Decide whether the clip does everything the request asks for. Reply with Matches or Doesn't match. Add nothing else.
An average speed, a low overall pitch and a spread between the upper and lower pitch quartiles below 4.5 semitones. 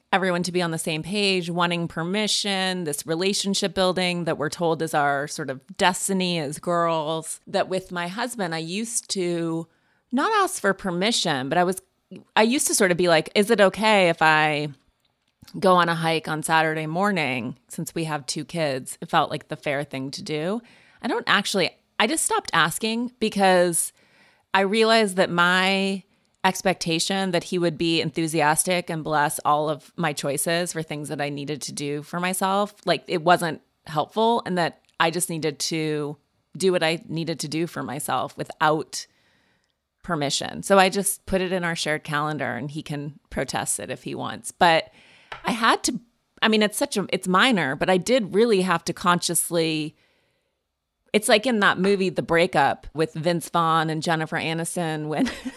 Doesn't match